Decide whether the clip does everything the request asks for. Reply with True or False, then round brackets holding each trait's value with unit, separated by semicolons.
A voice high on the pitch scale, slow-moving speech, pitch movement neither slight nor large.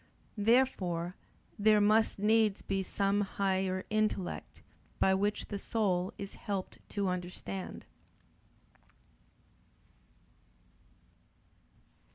False (195 Hz; 80 wpm; 2.1 semitones)